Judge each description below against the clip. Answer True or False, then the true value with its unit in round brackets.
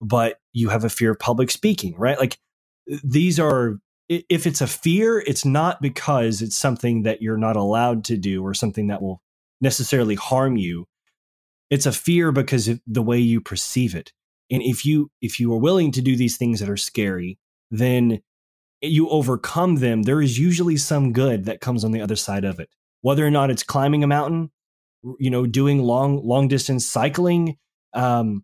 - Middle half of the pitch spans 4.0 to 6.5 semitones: True (4.3 semitones)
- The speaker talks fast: False (190 wpm)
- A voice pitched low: True (125 Hz)